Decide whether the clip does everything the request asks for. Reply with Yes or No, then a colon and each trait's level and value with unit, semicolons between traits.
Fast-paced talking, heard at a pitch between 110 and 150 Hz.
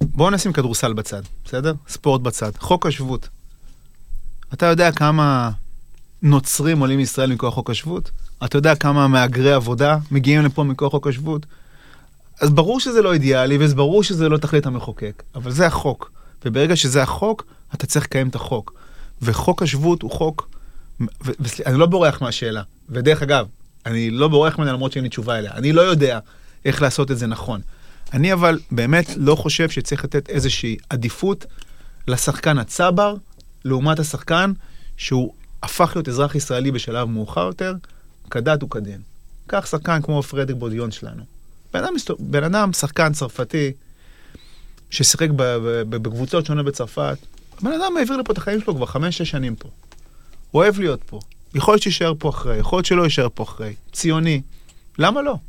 Yes: fast, 160 wpm; medium, 140 Hz